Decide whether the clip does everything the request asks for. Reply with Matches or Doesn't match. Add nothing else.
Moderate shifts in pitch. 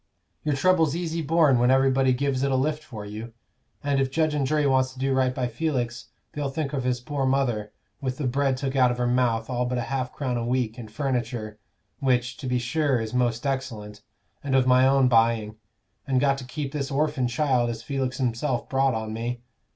Doesn't match